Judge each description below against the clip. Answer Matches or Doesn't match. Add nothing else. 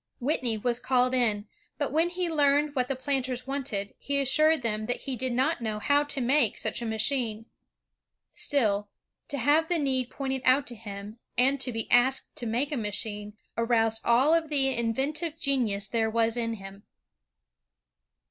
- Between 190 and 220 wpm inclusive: Doesn't match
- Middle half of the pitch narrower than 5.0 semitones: Matches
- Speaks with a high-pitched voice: Matches